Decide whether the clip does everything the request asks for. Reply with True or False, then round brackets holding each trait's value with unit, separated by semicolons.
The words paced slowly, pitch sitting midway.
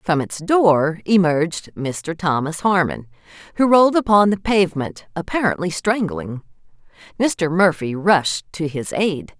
True (130 wpm; 170 Hz)